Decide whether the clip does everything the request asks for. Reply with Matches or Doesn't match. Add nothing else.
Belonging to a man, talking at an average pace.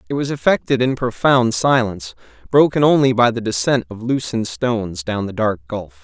Matches